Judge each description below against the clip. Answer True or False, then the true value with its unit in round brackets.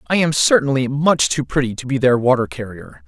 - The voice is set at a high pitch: False (135 Hz)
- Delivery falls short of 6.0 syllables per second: True (5.5 syllables/s)